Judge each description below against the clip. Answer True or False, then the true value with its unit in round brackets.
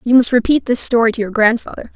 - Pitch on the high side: True (235 Hz)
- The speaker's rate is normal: False (245 wpm)